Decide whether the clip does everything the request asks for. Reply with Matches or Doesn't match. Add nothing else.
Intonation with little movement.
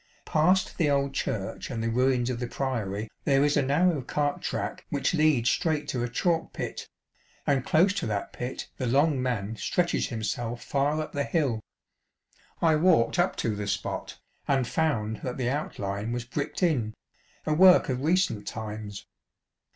Doesn't match